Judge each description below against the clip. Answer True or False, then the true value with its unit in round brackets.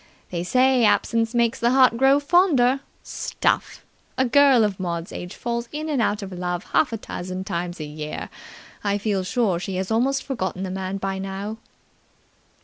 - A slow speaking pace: False (175 wpm)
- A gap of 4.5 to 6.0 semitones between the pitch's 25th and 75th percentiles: True (5.3 semitones)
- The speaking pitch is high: True (210 Hz)